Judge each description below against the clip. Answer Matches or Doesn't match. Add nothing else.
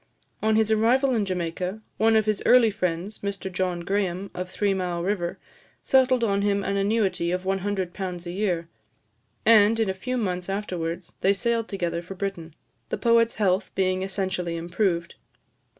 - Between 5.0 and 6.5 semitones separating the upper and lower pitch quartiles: Doesn't match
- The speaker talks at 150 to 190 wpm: Matches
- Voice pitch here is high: Matches